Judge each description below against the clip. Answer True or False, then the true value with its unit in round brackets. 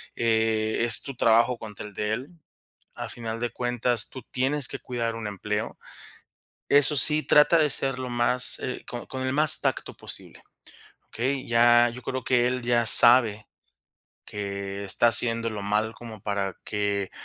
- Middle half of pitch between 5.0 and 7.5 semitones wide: False (2.8 semitones)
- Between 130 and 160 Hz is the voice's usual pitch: False (120 Hz)